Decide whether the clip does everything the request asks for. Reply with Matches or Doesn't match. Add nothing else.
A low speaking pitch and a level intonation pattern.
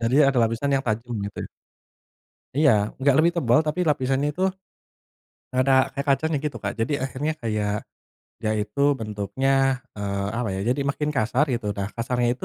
Doesn't match